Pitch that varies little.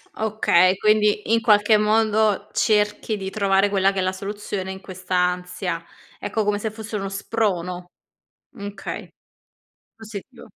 Yes: narrow, 2.2 semitones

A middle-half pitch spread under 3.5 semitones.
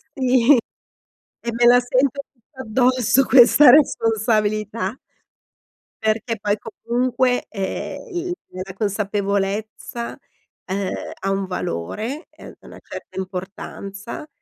No: average, 4.1 semitones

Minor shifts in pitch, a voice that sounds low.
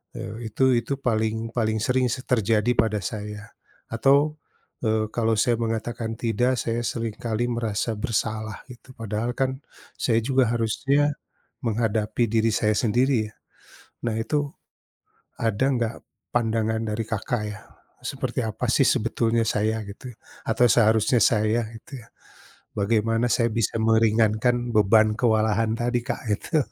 Yes: narrow, 1.9 semitones; low, 115 Hz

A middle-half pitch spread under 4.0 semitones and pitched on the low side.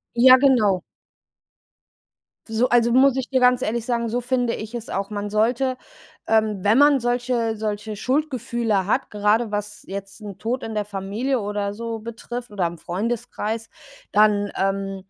No: average, 2.9 semitones; high, 225 Hz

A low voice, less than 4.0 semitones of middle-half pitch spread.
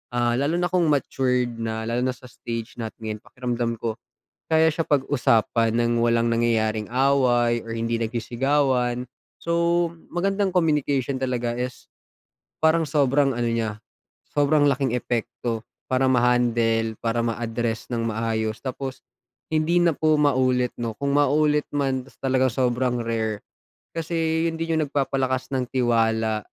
Yes: low, 125 Hz; average, 3.6 semitones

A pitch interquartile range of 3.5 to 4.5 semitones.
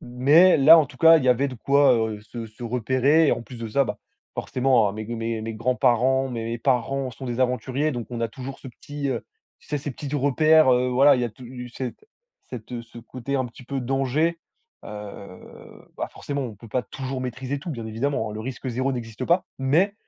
No: average, 3.0 semitones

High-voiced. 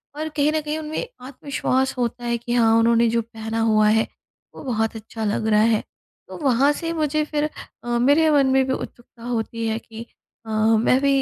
Yes: high, 240 Hz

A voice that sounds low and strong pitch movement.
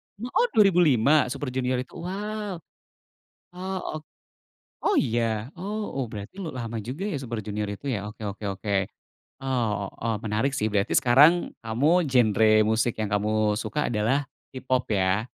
Yes: low, 125 Hz; wide, 6.7 semitones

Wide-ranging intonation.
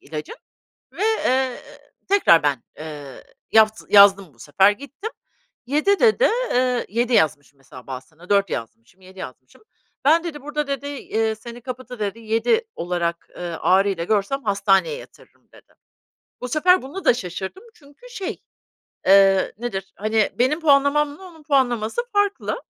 Yes: wide, 7.4 semitones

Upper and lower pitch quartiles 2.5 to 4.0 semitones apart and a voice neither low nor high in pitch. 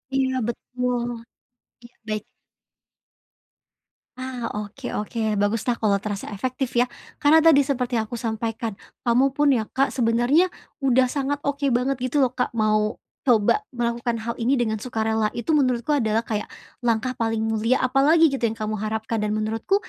No: average, 3.1 semitones; high, 240 Hz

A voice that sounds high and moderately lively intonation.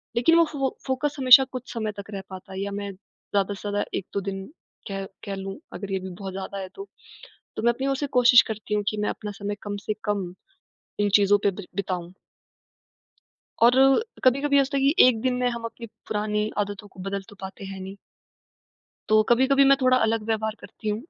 Yes: high, 210 Hz; average, 3.9 semitones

